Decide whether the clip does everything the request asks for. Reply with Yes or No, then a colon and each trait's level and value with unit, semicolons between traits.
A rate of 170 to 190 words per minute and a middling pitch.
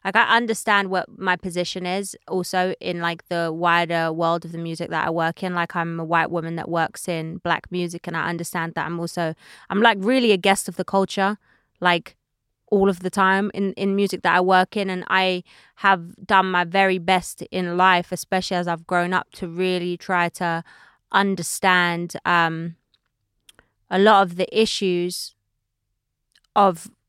Yes: average, 180 wpm; medium, 180 Hz